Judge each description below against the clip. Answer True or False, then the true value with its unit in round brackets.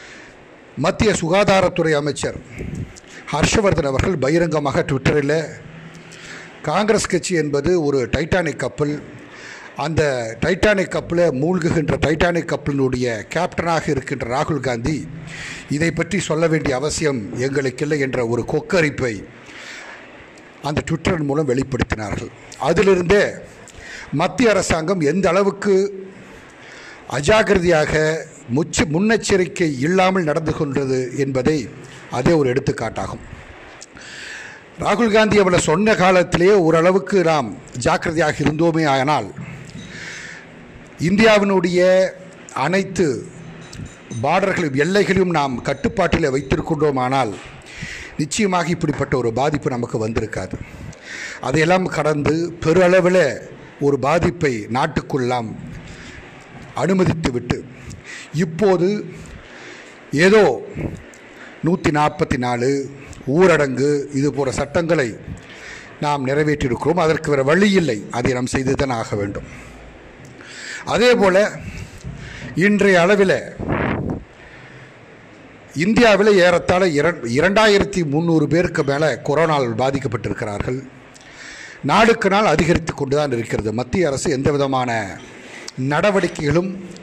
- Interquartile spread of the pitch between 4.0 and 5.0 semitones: True (4.7 semitones)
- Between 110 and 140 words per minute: False (85 wpm)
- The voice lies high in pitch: False (155 Hz)